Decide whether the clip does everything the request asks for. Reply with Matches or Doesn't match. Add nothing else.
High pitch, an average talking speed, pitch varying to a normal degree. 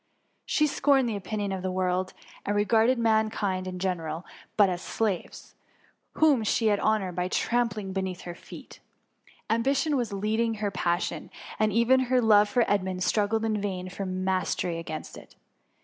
Matches